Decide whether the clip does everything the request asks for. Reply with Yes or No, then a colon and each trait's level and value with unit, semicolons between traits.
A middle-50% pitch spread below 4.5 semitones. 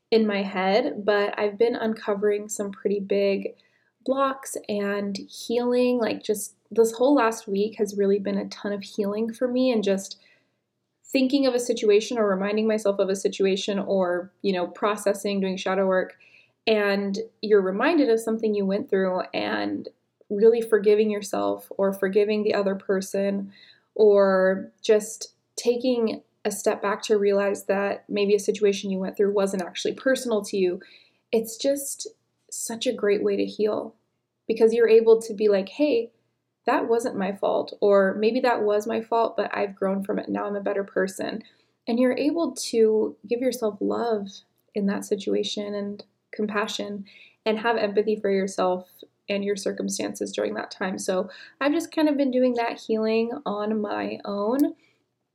Yes: narrow, 2.4 semitones